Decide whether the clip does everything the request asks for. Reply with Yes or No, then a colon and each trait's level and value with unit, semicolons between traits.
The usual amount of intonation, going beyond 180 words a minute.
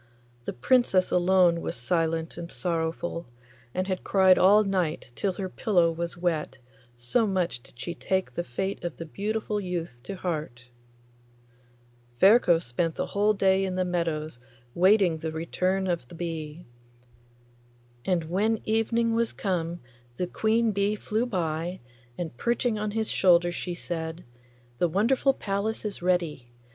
No: average, 3.4 semitones; average, 150 wpm